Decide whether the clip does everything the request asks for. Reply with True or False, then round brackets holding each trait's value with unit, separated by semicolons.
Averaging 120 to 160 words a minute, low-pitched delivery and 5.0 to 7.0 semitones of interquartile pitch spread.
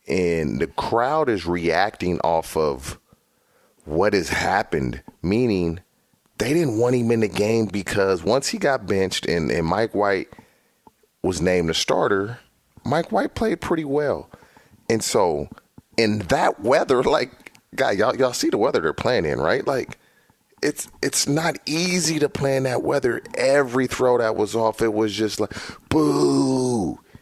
True (155 wpm; 110 Hz; 5.5 semitones)